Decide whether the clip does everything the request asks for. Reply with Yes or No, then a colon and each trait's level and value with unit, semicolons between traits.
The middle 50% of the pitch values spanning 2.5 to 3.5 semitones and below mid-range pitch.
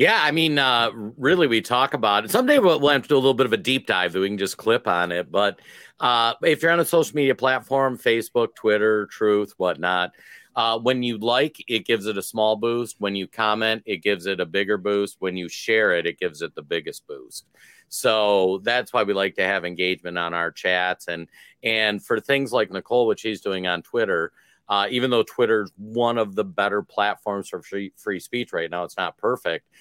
No: average, 4.9 semitones; low, 110 Hz